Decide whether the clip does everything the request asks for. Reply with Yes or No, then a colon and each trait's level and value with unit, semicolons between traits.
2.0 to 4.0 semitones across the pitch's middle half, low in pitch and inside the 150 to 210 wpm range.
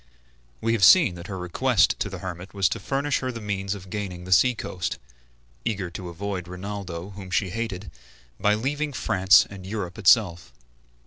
Yes: average, 3.0 semitones; very low, 95 Hz; average, 180 wpm